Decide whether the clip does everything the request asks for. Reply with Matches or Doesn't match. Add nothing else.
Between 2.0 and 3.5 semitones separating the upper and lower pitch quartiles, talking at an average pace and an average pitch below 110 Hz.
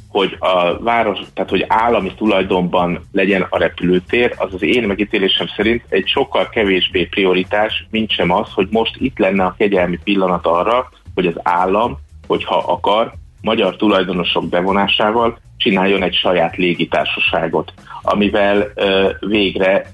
Matches